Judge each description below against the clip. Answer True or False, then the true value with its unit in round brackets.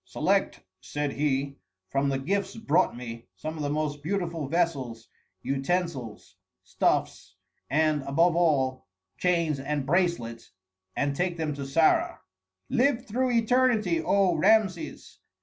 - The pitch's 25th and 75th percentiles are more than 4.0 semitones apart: True (4.6 semitones)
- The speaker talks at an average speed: False (125 wpm)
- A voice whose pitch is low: False (155 Hz)